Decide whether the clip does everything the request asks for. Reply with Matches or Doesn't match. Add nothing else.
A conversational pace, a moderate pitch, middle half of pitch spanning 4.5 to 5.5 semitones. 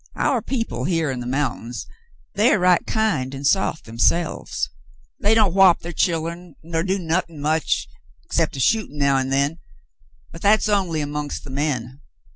Matches